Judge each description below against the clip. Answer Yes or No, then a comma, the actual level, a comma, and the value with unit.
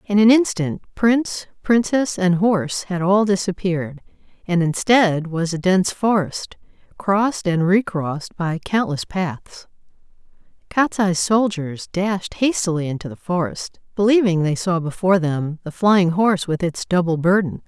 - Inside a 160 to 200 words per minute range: No, average, 140 wpm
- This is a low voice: No, medium, 185 Hz